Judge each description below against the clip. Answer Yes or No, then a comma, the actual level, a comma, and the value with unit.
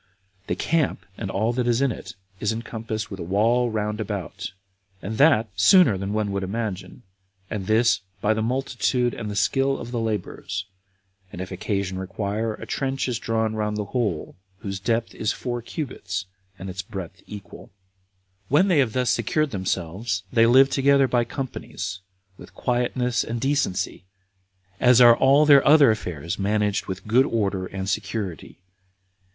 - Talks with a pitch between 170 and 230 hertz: No, low, 110 Hz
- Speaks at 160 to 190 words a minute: Yes, average, 165 wpm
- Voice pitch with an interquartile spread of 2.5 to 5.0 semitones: Yes, average, 4.0 semitones